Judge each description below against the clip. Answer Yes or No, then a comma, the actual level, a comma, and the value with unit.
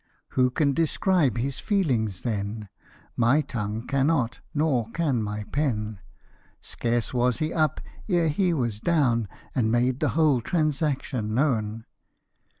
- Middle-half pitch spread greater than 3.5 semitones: Yes, average, 5.3 semitones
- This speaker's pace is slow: Yes, slow, 130 wpm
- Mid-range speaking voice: No, low, 125 Hz